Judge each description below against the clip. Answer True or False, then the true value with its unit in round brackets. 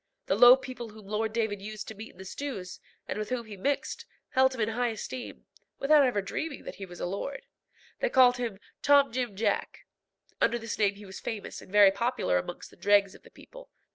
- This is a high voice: True (220 Hz)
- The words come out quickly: True (220 wpm)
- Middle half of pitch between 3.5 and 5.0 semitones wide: True (4.0 semitones)